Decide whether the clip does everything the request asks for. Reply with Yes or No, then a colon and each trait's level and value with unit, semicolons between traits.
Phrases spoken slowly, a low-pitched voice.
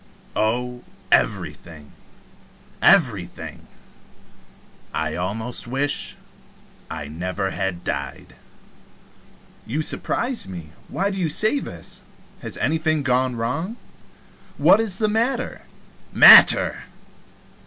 Yes: slow, 90 wpm; low, 125 Hz